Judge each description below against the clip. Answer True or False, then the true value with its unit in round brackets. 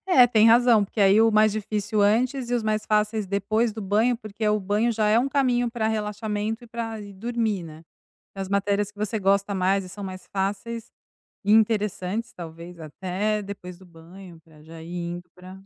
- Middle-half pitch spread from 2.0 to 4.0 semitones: True (2.8 semitones)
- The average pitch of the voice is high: True (210 Hz)